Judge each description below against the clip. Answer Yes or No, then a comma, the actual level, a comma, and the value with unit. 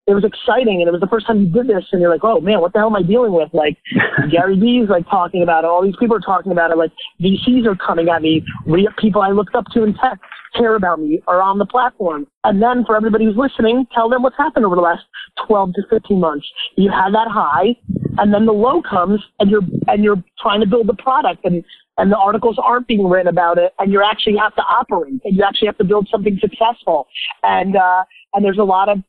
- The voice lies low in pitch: No, high, 205 Hz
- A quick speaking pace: Yes, fast, 255 wpm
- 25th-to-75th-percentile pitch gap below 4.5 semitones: Yes, average, 3.6 semitones